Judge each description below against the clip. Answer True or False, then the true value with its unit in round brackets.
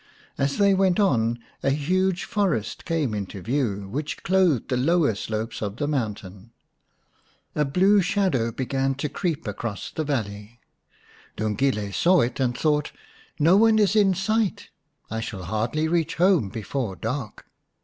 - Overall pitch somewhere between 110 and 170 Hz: True (140 Hz)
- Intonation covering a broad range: True (8.1 semitones)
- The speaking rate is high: False (150 wpm)